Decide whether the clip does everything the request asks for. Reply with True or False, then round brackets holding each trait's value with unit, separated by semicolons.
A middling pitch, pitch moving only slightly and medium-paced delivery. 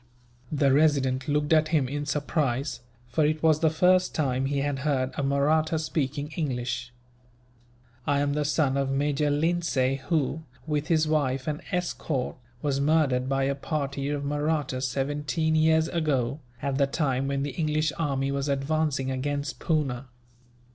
True (145 Hz; 2.3 semitones; 155 wpm)